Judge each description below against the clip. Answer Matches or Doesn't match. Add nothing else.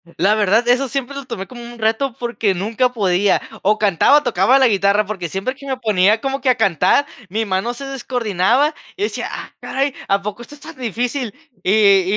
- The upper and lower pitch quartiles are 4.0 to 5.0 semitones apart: Matches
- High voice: Matches